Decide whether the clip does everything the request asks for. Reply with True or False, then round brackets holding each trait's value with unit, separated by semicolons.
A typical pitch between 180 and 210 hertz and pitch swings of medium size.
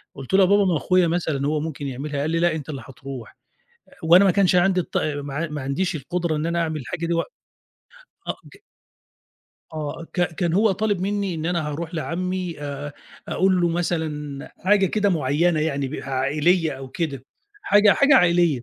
False (165 Hz; 3.8 semitones)